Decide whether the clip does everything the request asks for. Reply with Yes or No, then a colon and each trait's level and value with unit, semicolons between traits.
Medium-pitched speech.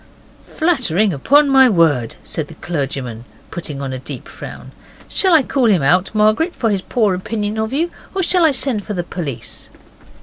No: high, 210 Hz